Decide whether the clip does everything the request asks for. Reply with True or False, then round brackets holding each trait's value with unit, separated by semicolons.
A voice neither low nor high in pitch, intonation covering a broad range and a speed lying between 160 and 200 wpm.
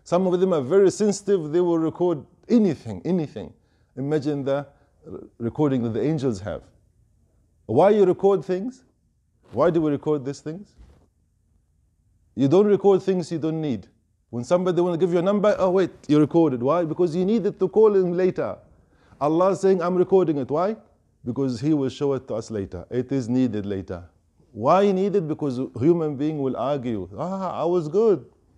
True (150 Hz; 7.9 semitones; 180 wpm)